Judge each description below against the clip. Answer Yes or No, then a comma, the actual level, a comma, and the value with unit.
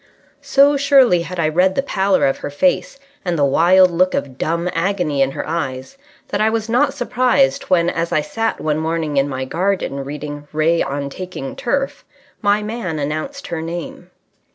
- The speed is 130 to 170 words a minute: No, average, 180 wpm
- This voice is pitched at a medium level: Yes, medium, 170 Hz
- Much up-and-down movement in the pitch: Yes, wide, 6.5 semitones